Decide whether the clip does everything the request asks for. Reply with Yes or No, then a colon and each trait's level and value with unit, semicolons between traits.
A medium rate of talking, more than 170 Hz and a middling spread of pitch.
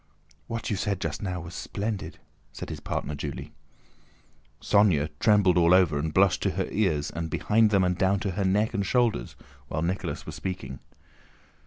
No: average, 175 wpm; very low, 95 Hz; average, 3.8 semitones